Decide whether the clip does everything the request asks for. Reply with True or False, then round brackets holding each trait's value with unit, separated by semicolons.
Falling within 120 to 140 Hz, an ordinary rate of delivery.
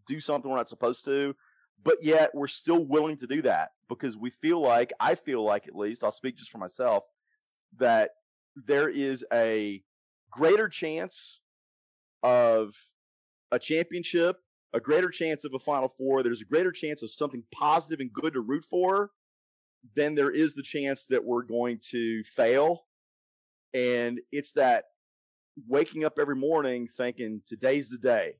True (135 Hz; 165 wpm)